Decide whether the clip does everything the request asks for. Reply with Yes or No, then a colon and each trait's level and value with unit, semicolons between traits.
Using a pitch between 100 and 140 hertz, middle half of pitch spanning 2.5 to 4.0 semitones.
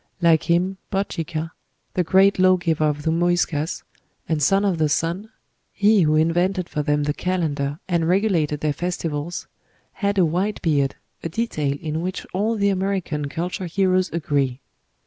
No: medium, 170 Hz; average, 3.5 semitones